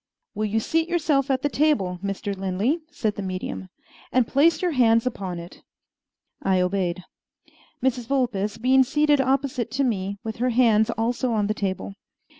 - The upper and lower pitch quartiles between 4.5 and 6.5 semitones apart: Yes, average, 5.2 semitones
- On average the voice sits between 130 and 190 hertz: No, high, 230 Hz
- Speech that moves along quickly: No, average, 170 wpm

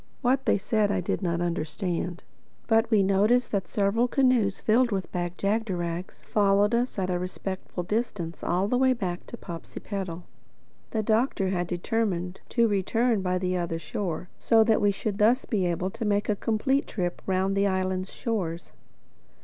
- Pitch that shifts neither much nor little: Yes, average, 3.7 semitones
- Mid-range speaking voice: No, high, 195 Hz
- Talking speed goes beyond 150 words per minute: Yes, average, 170 wpm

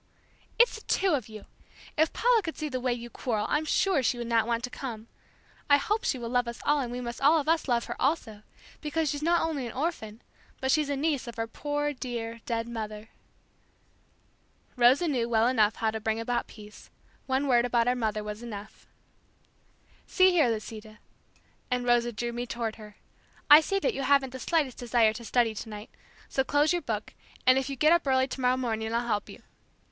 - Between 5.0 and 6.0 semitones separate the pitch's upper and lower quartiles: No, average, 4.1 semitones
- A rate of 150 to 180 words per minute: No, fast, 205 wpm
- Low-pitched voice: No, high, 245 Hz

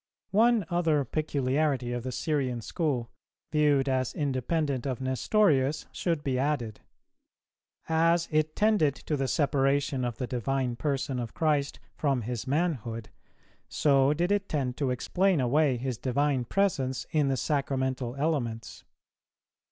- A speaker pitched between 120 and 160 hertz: Yes, medium, 140 Hz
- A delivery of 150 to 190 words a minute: No, slow, 135 wpm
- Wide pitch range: No, average, 3.3 semitones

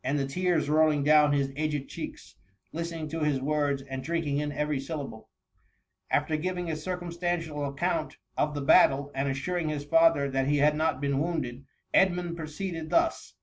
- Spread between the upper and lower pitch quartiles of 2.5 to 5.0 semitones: Yes, average, 2.9 semitones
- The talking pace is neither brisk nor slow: Yes, average, 170 wpm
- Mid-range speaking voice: Yes, medium, 150 Hz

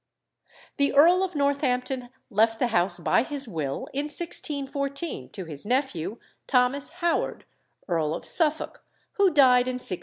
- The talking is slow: No, average, 145 wpm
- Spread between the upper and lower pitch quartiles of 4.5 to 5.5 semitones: Yes, average, 5.1 semitones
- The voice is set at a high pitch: Yes, very high, 265 Hz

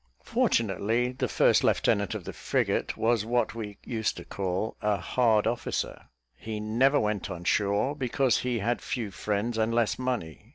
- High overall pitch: No, low, 110 Hz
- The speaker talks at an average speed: Yes, average, 165 wpm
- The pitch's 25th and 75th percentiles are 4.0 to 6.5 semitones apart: No, average, 2.7 semitones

